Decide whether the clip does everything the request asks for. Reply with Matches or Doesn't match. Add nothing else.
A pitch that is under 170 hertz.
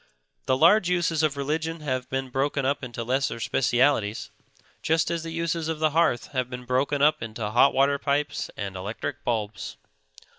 Matches